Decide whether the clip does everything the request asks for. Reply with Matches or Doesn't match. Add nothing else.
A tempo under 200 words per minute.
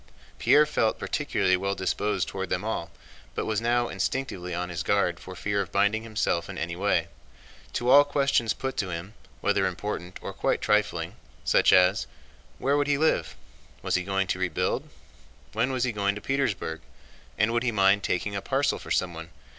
Matches